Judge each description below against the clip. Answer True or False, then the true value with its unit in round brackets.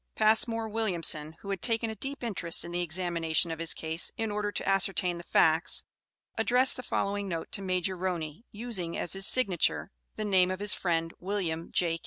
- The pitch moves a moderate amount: True (3.9 semitones)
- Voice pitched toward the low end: False (185 Hz)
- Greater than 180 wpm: True (190 wpm)